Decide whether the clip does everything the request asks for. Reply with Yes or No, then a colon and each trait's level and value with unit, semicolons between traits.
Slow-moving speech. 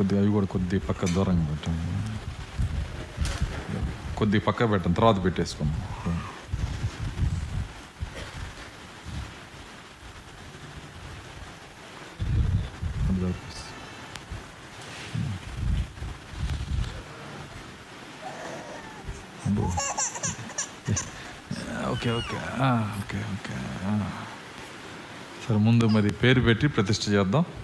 Yes: slow, 40 wpm